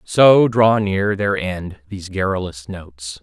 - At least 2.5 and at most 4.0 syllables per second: Yes, 3.9 syllables/s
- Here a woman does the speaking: No, male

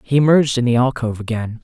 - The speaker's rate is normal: No, fast, 220 wpm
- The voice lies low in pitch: Yes, low, 125 Hz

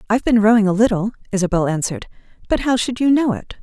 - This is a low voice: No, high, 215 Hz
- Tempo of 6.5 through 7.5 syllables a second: Yes, 7.1 syllables/s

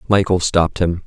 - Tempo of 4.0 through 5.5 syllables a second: No, 5.7 syllables/s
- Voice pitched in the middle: No, very low, 85 Hz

